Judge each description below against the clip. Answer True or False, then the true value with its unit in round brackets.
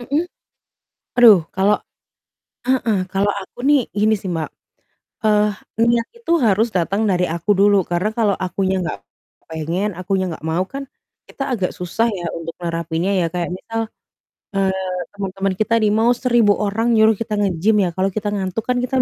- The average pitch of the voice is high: True (200 Hz)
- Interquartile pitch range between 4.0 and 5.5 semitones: False (3.4 semitones)